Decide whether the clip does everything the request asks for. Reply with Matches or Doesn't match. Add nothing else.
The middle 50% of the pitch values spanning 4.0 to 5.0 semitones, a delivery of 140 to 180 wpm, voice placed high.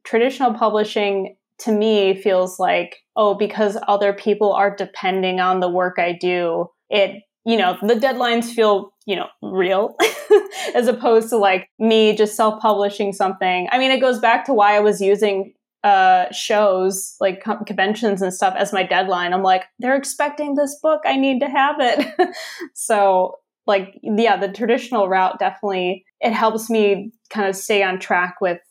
Doesn't match